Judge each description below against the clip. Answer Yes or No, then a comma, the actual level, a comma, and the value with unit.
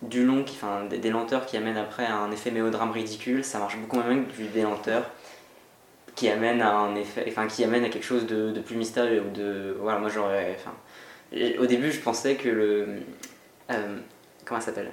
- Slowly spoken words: No, average, 215 wpm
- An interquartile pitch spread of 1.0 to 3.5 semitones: Yes, narrow, 2.5 semitones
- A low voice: Yes, low, 110 Hz